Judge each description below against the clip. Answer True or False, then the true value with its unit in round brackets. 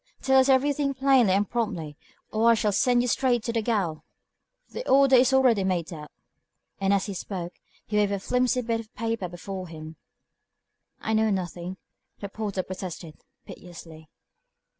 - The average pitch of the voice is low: False (210 Hz)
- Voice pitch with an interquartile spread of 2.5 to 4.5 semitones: False (5.2 semitones)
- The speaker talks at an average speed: True (160 wpm)